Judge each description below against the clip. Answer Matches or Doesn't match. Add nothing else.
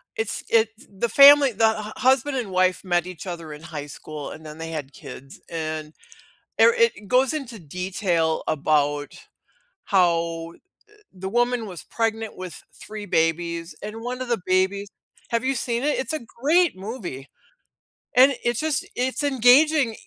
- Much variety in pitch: Matches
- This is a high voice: Matches